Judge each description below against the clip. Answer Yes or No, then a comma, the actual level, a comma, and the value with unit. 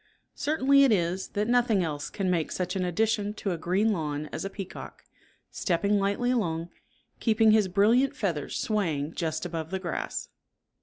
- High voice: Yes, high, 195 Hz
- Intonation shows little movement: No, average, 4.5 semitones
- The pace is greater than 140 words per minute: Yes, average, 165 wpm